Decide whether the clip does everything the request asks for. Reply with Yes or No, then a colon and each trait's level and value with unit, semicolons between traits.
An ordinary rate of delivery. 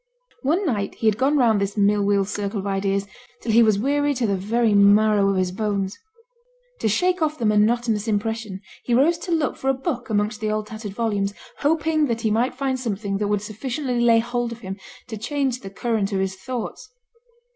No: fast, 210 wpm